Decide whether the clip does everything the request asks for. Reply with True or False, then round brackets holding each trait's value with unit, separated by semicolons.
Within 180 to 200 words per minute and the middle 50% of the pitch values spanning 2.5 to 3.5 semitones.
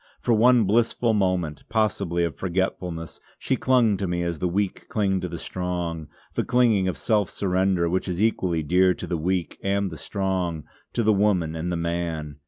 True (190 wpm; 3.0 semitones)